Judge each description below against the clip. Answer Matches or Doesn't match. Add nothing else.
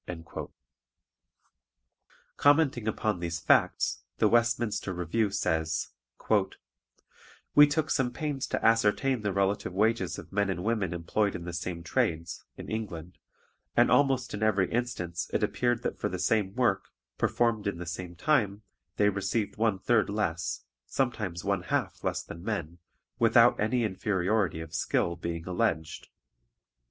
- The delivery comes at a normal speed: Matches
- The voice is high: Doesn't match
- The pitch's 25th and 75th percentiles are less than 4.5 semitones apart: Doesn't match